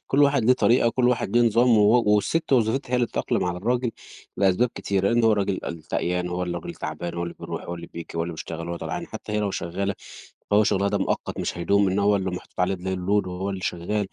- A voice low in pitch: Yes, low, 100 Hz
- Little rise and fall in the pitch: No, average, 4.3 semitones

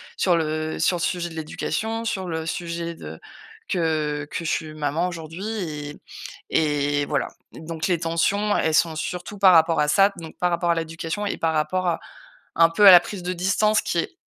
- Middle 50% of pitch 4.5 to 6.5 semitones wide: No, narrow, 2.6 semitones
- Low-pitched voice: No, medium, 165 Hz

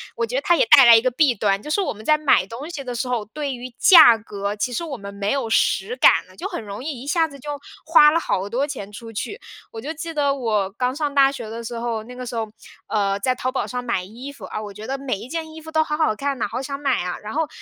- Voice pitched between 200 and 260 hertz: Yes, very high, 250 Hz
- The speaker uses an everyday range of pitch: Yes, average, 4.9 semitones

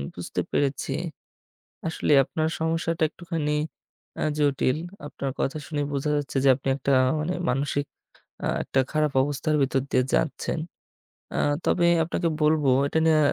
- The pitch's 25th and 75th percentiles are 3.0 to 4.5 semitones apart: No, narrow, 2.5 semitones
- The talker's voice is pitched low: No, medium, 150 Hz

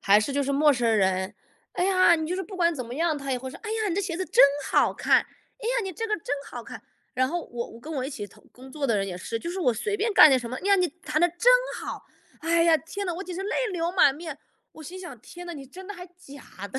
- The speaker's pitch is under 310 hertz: No, very high, 320 Hz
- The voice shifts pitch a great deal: Yes, wide, 5.8 semitones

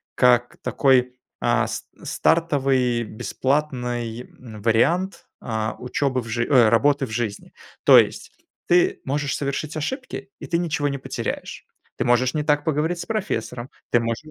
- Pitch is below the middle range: Yes, low, 130 Hz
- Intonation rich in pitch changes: No, average, 3.8 semitones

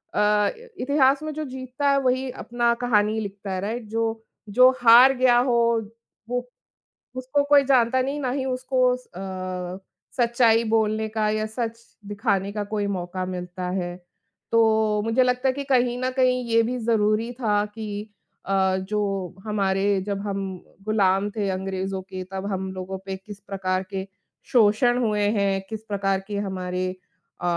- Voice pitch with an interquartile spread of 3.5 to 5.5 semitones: Yes, average, 4.2 semitones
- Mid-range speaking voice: No, high, 215 Hz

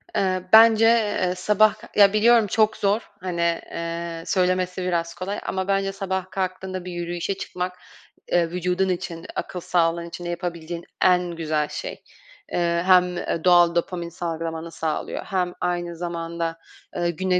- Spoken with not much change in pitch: Yes, narrow, 1.9 semitones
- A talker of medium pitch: Yes, medium, 180 Hz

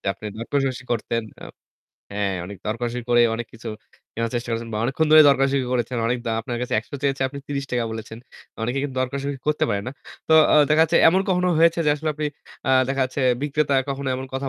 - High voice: No, low, 130 Hz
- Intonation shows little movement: No, average, 3.4 semitones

